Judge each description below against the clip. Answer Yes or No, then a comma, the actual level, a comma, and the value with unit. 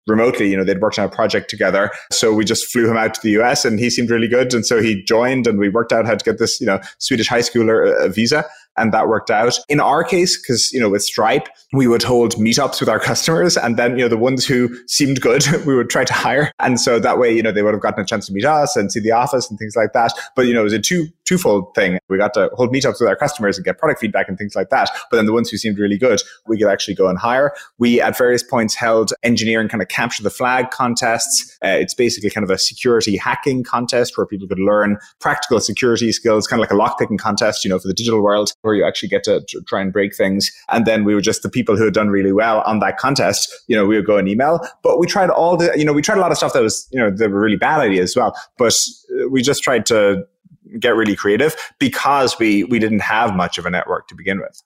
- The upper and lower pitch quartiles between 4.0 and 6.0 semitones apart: No, average, 3.4 semitones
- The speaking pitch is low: Yes, low, 115 Hz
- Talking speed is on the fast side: Yes, fast, 275 wpm